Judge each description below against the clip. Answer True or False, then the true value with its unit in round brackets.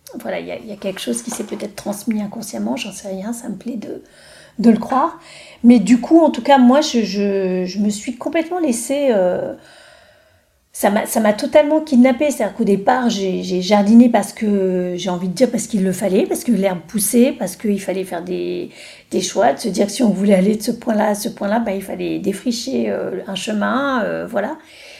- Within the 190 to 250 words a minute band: True (220 wpm)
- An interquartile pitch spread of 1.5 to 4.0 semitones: False (4.5 semitones)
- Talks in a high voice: True (215 Hz)